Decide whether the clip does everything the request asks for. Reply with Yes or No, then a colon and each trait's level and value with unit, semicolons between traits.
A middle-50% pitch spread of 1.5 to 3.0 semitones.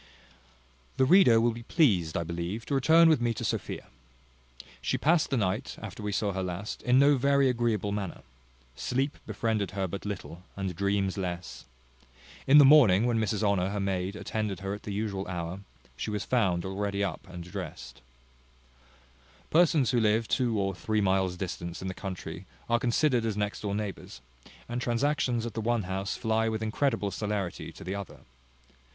No: average, 3.7 semitones